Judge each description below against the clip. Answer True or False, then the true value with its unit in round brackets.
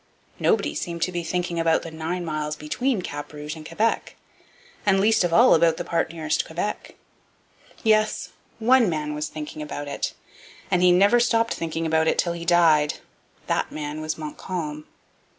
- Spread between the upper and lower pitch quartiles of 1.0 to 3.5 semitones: True (2.9 semitones)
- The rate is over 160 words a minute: True (170 wpm)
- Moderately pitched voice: True (165 Hz)